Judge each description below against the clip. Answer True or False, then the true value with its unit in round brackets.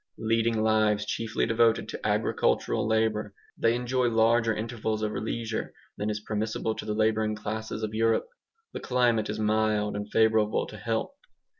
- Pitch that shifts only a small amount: True (1.1 semitones)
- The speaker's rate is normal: True (155 wpm)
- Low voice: True (110 Hz)